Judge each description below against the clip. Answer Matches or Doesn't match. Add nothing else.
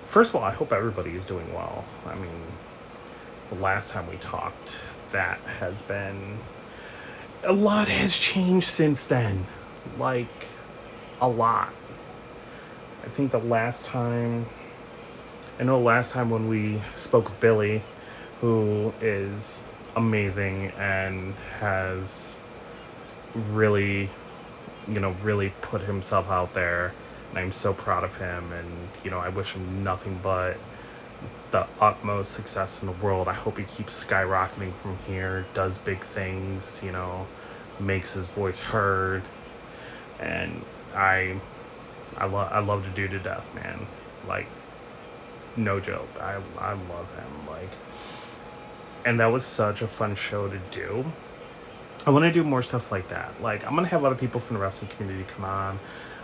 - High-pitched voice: Doesn't match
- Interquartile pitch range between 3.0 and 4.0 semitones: Matches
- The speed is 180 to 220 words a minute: Doesn't match